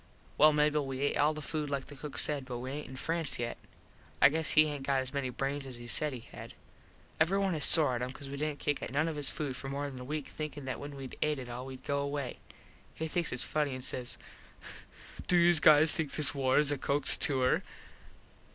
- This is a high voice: No, medium, 145 Hz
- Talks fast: Yes, fast, 245 wpm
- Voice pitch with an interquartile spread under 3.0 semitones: Yes, narrow, 2.5 semitones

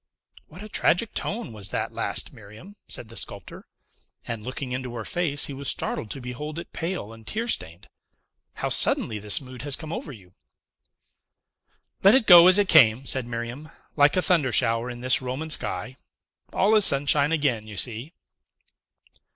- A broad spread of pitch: Yes, wide, 6.0 semitones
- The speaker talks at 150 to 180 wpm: Yes, average, 175 wpm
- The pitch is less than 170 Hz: Yes, low, 135 Hz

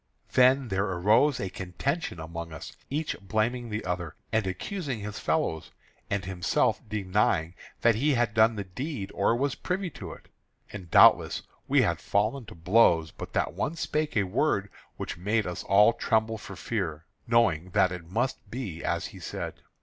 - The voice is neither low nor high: No, low, 105 Hz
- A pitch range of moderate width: Yes, average, 4.9 semitones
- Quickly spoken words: No, average, 175 wpm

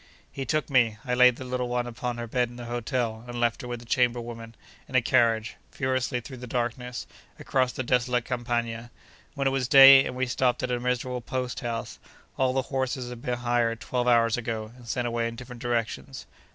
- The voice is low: Yes, low, 125 Hz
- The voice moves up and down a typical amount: No, narrow, 1.4 semitones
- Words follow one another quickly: Yes, fast, 215 wpm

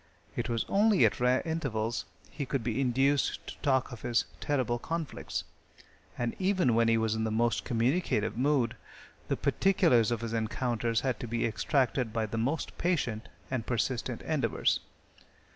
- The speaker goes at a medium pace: Yes, average, 160 wpm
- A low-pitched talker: Yes, low, 120 Hz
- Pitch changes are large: No, average, 3.4 semitones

